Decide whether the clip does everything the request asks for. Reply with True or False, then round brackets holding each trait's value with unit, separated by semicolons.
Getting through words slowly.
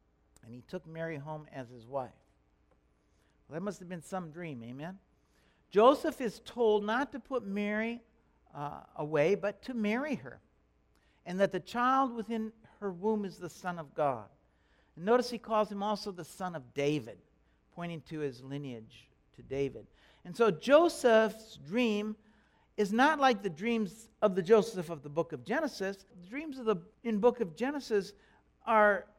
False (175 wpm)